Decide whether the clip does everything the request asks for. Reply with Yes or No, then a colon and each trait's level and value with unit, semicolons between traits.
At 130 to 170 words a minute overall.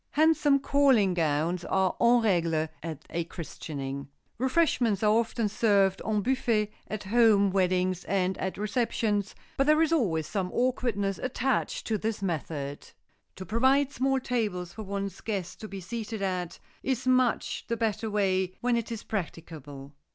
Yes: average, 150 wpm